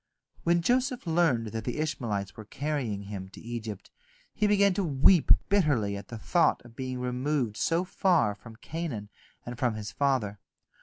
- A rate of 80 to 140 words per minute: No, average, 165 wpm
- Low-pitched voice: Yes, low, 125 Hz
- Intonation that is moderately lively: No, wide, 7.4 semitones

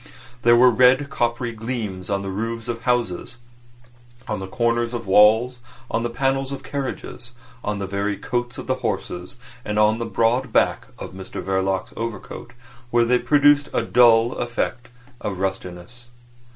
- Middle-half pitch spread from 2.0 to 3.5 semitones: Yes, average, 3.0 semitones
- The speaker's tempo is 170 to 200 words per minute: No, average, 160 wpm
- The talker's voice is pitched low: Yes, low, 115 Hz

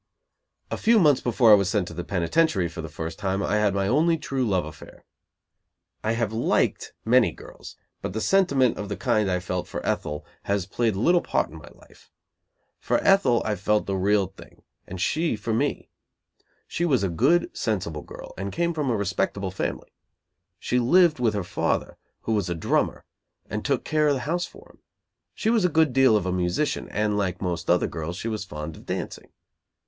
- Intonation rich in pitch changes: Yes, wide, 7.1 semitones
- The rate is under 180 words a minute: No, average, 200 wpm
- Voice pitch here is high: No, low, 105 Hz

